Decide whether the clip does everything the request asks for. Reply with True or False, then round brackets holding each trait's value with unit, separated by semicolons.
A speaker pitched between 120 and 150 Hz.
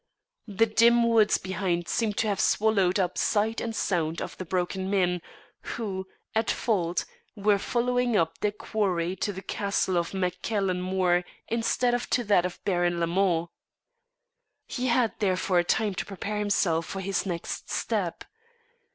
False (195 Hz)